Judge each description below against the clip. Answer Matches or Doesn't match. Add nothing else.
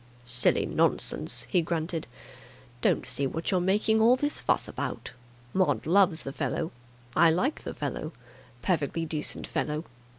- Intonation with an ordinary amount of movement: Matches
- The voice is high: Doesn't match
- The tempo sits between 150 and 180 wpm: Doesn't match